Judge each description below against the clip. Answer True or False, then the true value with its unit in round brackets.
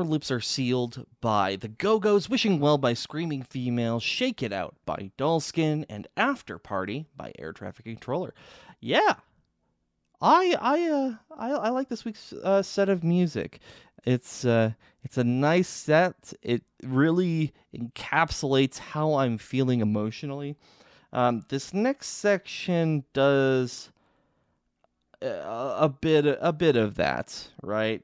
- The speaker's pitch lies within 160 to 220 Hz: False (140 Hz)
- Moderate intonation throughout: False (6.9 semitones)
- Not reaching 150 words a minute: True (135 wpm)